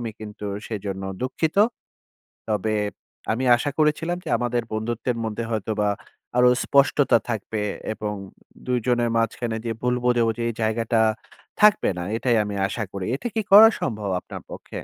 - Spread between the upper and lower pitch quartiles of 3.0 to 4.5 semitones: No, narrow, 2.4 semitones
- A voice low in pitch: Yes, low, 115 Hz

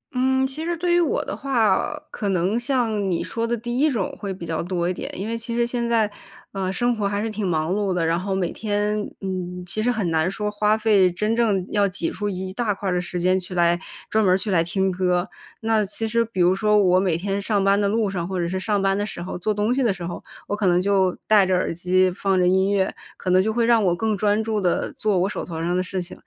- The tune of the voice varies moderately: Yes, average, 3.1 semitones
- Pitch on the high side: Yes, high, 200 Hz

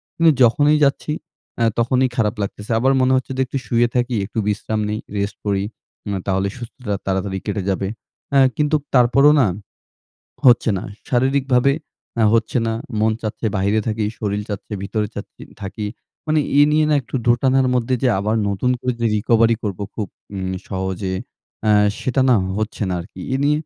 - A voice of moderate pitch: No, low, 115 Hz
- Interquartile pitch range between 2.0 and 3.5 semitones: No, average, 4.2 semitones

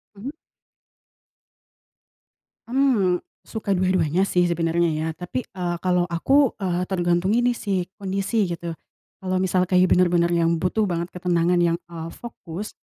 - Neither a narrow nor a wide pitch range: No, narrow, 2.3 semitones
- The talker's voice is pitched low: No, medium, 180 Hz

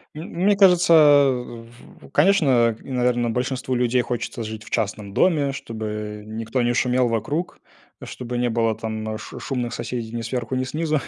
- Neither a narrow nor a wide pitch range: Yes, average, 3.2 semitones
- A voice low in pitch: Yes, low, 120 Hz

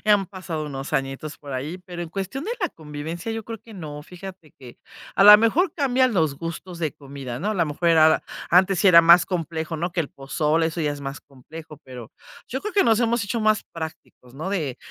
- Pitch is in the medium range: Yes, medium, 165 Hz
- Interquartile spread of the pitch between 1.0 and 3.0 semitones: No, average, 5.3 semitones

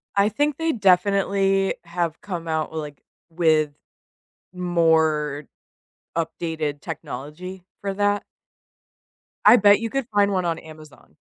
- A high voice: No, medium, 175 Hz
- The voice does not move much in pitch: No, average, 4.1 semitones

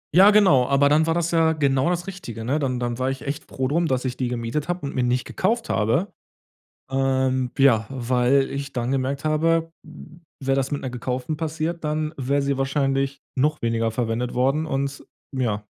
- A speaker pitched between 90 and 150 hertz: Yes, low, 135 Hz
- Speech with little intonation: No, average, 3.6 semitones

